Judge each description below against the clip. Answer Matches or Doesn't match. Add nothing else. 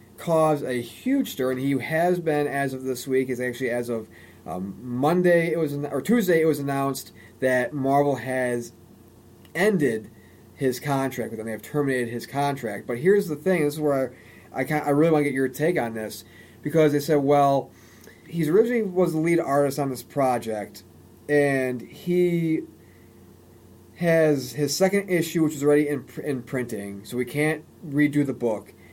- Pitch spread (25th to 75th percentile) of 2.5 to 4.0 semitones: Doesn't match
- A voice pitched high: Doesn't match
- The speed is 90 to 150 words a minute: Doesn't match